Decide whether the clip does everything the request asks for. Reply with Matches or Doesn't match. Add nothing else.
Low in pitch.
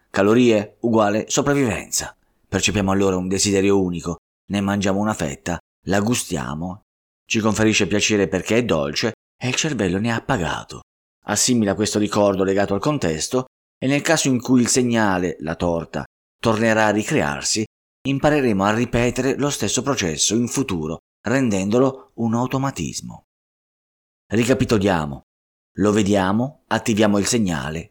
Matches